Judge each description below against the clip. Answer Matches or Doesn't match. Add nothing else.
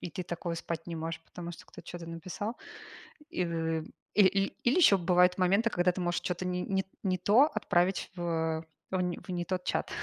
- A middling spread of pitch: Doesn't match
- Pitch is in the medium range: Matches